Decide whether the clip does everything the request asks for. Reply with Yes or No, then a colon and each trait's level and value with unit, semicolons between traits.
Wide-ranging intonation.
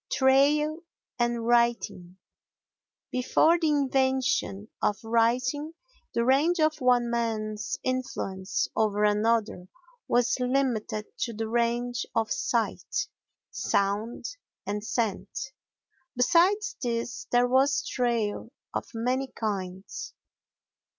No: average, 3.4 semitones